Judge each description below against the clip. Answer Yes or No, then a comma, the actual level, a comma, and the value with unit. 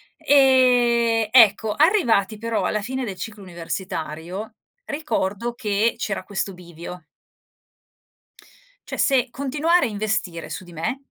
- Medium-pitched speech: No, high, 220 Hz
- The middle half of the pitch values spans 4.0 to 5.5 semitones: Yes, average, 5.1 semitones